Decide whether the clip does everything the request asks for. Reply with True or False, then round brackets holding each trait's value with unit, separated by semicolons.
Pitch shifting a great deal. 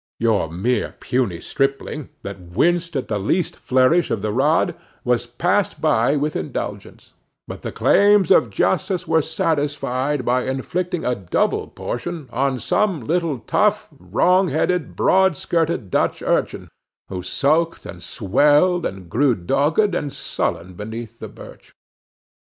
True (6.5 semitones)